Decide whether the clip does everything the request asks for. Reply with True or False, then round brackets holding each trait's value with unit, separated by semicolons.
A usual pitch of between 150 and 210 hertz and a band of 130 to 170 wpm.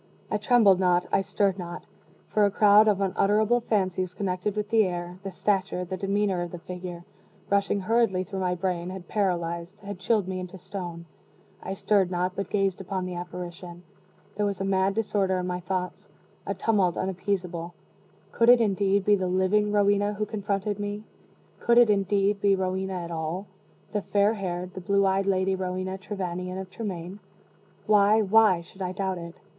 False (190 Hz; 180 wpm)